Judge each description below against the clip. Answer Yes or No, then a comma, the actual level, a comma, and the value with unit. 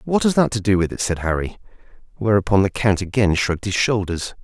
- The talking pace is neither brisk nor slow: No, fast, 215 wpm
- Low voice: Yes, low, 105 Hz